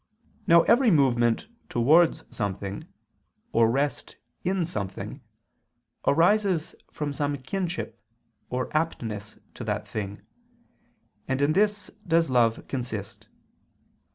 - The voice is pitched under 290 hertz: Yes, medium, 140 Hz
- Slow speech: Yes, slow, 100 wpm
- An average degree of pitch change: No, wide, 6.6 semitones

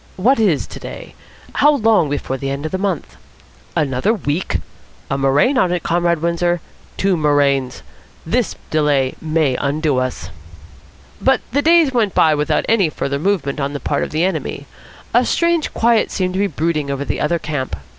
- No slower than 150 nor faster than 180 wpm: Yes, average, 175 wpm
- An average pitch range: No, wide, 5.7 semitones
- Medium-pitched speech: Yes, medium, 160 Hz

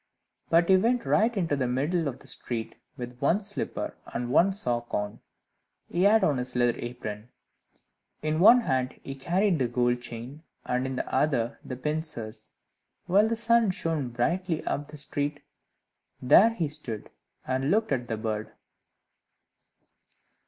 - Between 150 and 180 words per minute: Yes, average, 155 wpm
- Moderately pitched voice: Yes, medium, 145 Hz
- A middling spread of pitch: No, wide, 6.9 semitones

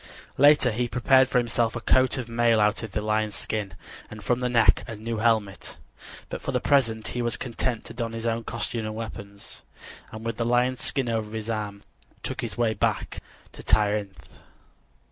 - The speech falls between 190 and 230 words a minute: Yes, average, 195 wpm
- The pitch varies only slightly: Yes, narrow, 2.0 semitones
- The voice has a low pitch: Yes, low, 115 Hz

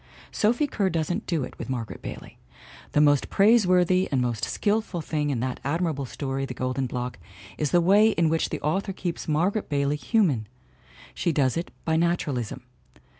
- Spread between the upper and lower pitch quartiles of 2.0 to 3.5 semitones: No, average, 5.3 semitones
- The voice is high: No, medium, 155 Hz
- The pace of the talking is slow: No, average, 175 wpm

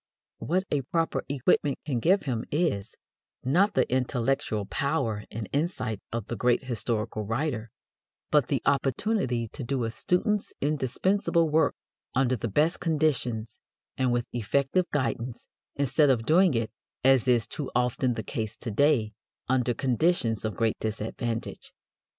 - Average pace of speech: Yes, average, 145 wpm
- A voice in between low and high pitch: No, low, 130 Hz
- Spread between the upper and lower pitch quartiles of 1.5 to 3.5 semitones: No, average, 4.6 semitones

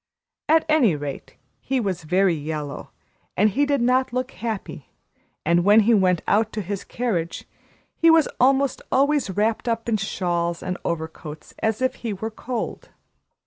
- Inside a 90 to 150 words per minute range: No, average, 160 wpm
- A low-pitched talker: No, high, 215 Hz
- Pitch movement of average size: No, wide, 6.5 semitones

